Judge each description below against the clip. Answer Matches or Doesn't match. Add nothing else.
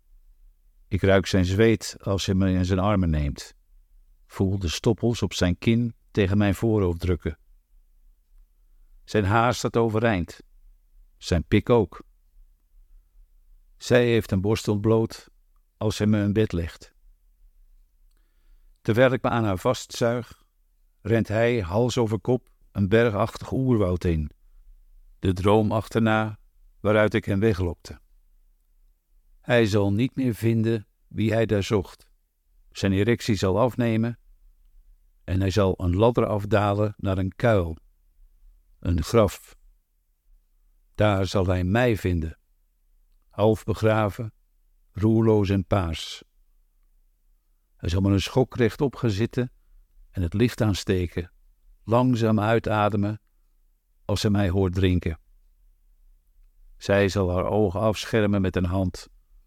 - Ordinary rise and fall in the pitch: Doesn't match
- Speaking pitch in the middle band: Doesn't match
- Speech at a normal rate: Doesn't match